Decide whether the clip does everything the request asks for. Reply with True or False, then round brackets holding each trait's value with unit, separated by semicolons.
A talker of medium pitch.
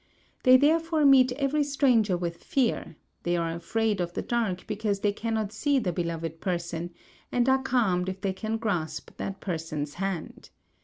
False (205 Hz)